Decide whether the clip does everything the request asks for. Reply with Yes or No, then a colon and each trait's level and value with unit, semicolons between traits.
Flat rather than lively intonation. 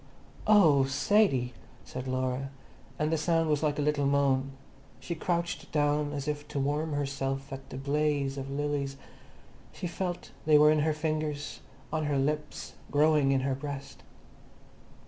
Yes: narrow, 1.9 semitones